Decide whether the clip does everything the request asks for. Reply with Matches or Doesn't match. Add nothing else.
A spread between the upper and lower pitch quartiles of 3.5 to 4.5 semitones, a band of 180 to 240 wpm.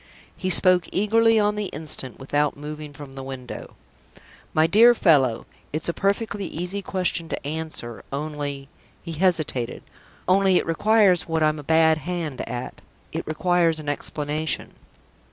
Doesn't match